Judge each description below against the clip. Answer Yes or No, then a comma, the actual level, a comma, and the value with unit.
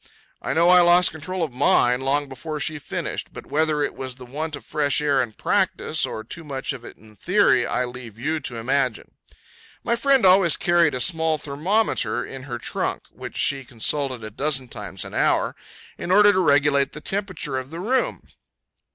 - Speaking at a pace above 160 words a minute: Yes, average, 195 wpm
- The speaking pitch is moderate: Yes, medium, 145 Hz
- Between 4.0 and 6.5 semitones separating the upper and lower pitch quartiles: Yes, average, 4.7 semitones